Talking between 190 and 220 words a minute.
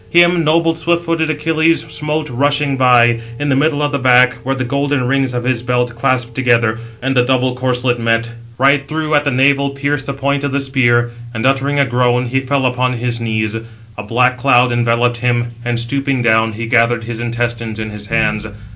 Yes: average, 200 wpm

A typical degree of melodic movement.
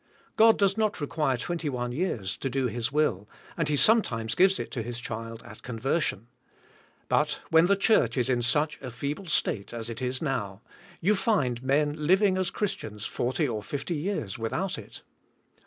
No: wide, 6.8 semitones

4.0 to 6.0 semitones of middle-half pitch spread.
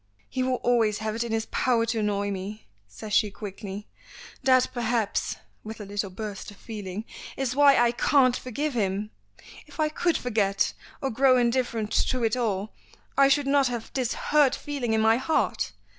No: average, 3.5 semitones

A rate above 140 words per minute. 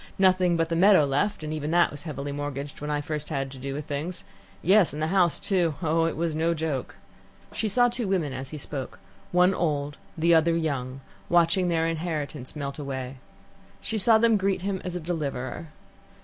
Yes: average, 200 wpm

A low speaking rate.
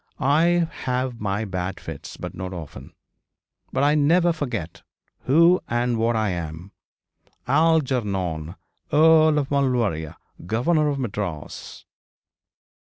Yes: slow, 110 wpm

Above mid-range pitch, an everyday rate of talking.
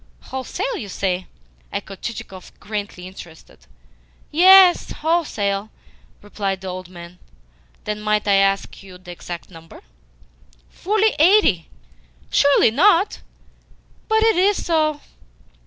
No: high, 210 Hz; slow, 110 wpm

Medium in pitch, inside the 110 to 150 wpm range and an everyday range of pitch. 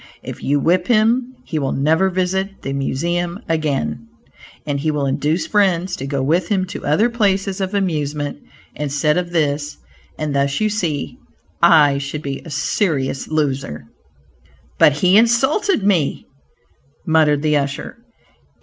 Yes: medium, 160 Hz; average, 145 wpm; average, 4.9 semitones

